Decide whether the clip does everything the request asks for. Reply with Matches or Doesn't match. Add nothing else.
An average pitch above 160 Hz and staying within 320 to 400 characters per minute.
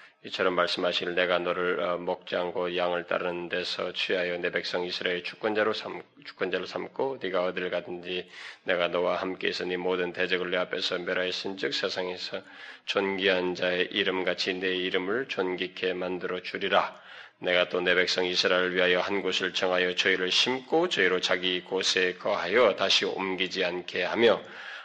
Doesn't match